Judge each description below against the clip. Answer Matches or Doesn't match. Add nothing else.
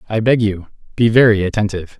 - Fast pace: Doesn't match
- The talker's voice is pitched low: Matches